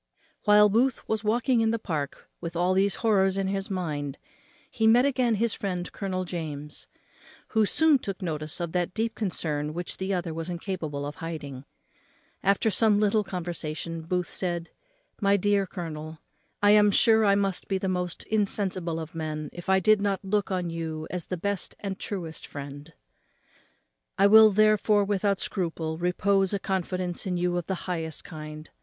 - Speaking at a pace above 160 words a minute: Yes, average, 175 wpm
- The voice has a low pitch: No, medium, 185 Hz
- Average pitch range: Yes, average, 3.7 semitones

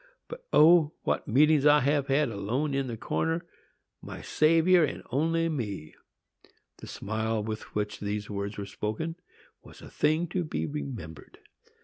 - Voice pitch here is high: No, medium, 140 Hz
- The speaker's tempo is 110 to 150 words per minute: Yes, average, 145 wpm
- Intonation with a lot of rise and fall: Yes, wide, 6.9 semitones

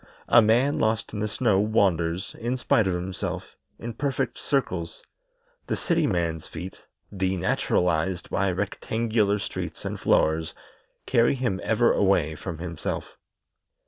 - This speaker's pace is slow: Yes, slow, 130 wpm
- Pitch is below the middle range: Yes, low, 100 Hz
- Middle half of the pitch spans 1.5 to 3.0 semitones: No, average, 4.7 semitones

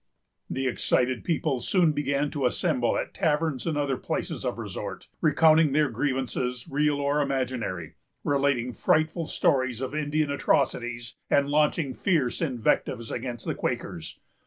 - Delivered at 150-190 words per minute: No, slow, 135 wpm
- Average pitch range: Yes, average, 3.2 semitones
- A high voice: No, medium, 140 Hz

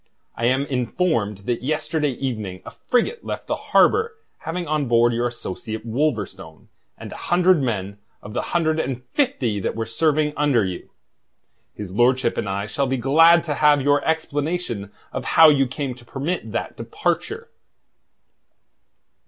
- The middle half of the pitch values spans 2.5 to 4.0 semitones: No, wide, 5.6 semitones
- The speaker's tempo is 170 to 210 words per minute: No, average, 155 wpm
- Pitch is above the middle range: No, low, 135 Hz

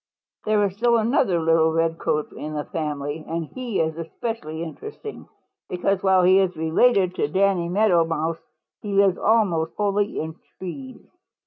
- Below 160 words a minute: Yes, average, 150 wpm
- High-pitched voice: No, medium, 180 Hz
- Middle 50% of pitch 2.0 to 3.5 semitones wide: No, average, 4.3 semitones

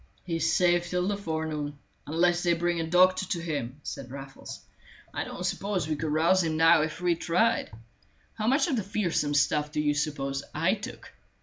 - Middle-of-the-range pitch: Yes, medium, 165 Hz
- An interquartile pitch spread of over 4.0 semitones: No, average, 3.1 semitones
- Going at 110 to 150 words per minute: No, average, 195 wpm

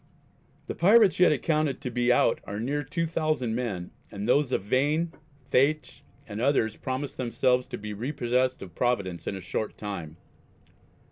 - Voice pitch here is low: Yes, low, 125 Hz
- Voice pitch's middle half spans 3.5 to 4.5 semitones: No, wide, 5.5 semitones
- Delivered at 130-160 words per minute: Yes, average, 155 wpm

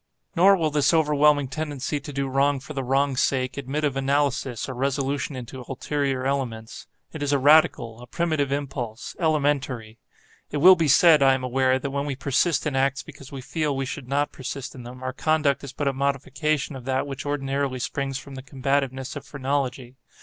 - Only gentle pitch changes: Yes, narrow, 1.8 semitones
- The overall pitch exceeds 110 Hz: Yes, medium, 140 Hz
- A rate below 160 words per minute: No, average, 195 wpm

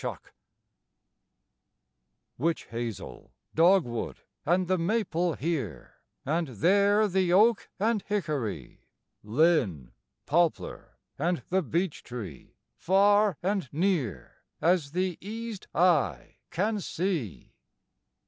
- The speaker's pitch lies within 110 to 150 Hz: No, medium, 175 Hz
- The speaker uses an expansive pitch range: Yes, wide, 5.7 semitones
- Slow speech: Yes, slow, 100 wpm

